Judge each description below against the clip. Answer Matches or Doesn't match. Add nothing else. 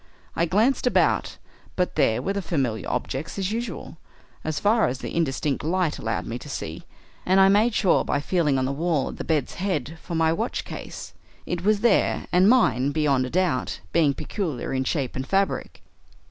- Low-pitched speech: Doesn't match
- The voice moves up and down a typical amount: Doesn't match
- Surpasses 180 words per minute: Matches